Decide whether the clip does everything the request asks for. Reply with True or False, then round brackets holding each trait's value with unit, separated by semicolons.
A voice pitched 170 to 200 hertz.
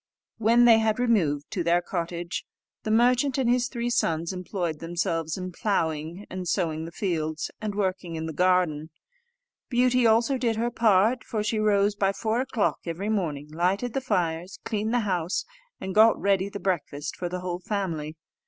True (190 Hz)